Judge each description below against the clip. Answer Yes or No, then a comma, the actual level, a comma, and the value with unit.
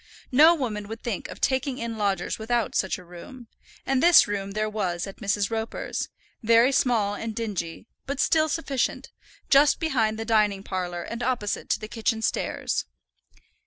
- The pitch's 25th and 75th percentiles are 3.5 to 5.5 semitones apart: Yes, average, 3.9 semitones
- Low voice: No, high, 225 Hz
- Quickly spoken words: No, average, 165 wpm